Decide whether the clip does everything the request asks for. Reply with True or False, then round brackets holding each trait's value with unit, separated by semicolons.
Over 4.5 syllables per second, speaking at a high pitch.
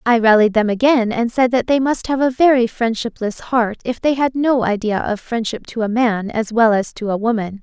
True (5.1 syllables/s; 235 Hz)